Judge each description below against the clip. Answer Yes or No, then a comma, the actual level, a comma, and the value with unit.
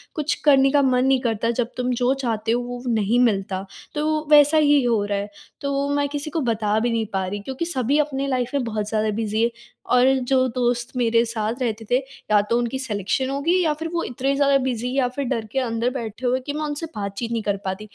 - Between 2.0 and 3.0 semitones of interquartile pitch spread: No, average, 3.7 semitones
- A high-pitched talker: Yes, high, 245 Hz